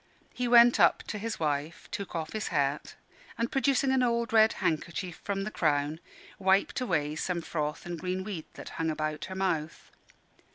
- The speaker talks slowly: No, average, 175 wpm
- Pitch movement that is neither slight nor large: No, wide, 6.0 semitones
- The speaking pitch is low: No, medium, 180 Hz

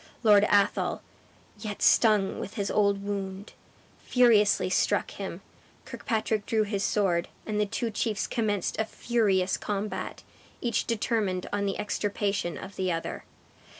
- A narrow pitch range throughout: Yes, narrow, 1.6 semitones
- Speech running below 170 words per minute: Yes, slow, 135 wpm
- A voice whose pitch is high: Yes, high, 205 Hz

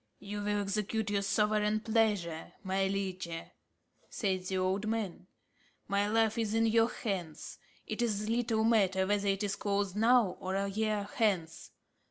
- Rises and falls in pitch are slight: Yes, narrow, 2.2 semitones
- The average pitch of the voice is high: Yes, high, 205 Hz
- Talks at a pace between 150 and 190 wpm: Yes, average, 155 wpm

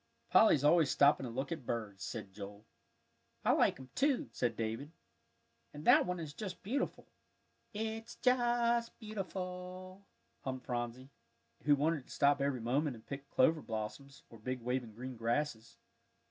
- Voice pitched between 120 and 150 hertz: Yes, medium, 140 Hz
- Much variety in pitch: Yes, wide, 7.2 semitones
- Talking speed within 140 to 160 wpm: Yes, average, 155 wpm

